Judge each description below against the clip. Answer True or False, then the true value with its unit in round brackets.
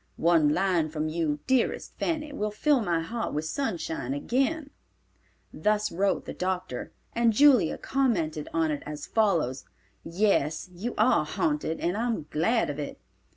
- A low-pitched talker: False (185 Hz)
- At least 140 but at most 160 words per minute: True (155 wpm)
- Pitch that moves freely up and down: True (7.1 semitones)